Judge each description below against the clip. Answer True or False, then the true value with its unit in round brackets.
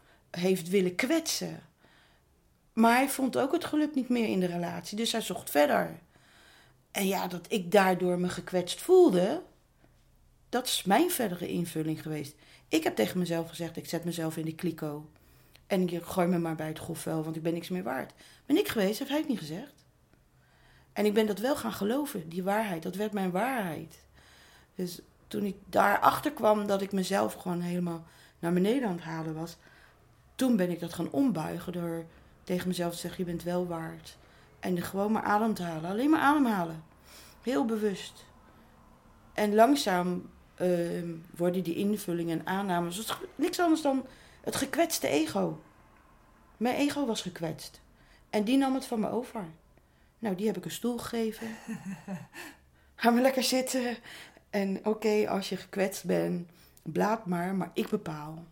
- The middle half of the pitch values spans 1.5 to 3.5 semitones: False (5.0 semitones)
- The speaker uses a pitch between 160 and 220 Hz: True (190 Hz)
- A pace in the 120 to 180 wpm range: True (170 wpm)